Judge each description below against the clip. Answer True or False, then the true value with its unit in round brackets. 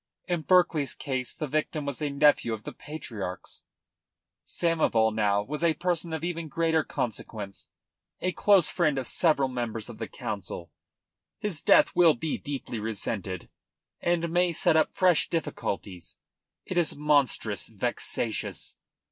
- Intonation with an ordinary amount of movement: False (6.8 semitones)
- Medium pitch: True (145 Hz)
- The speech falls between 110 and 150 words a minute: True (140 wpm)